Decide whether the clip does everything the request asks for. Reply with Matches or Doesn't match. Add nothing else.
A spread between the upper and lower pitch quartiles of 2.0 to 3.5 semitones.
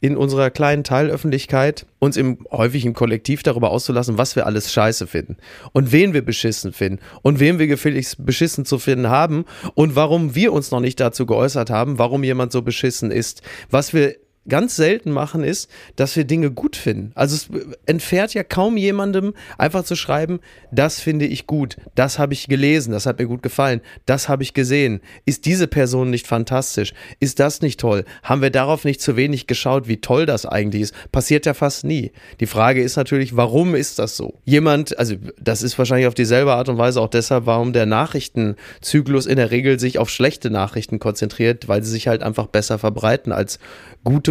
Doesn't match